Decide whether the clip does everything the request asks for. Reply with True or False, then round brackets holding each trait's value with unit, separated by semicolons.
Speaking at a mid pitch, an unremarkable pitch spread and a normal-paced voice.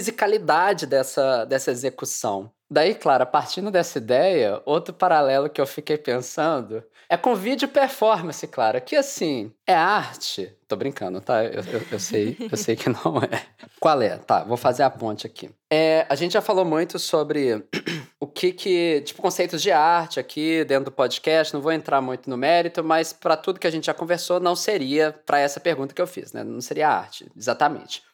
True (160 Hz; 4.5 semitones; 190 wpm)